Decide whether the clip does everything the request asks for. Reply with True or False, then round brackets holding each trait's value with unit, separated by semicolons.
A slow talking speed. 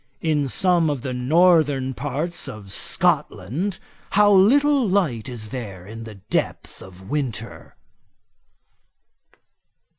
True (110 wpm)